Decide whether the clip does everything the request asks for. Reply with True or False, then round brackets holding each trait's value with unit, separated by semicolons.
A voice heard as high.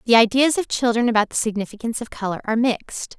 True (230 Hz)